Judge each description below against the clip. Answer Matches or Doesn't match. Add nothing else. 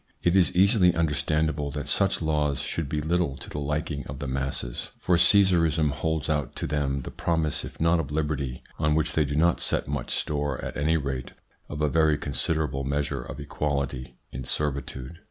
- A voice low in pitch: Matches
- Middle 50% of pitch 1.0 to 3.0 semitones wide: Matches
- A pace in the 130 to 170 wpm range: Doesn't match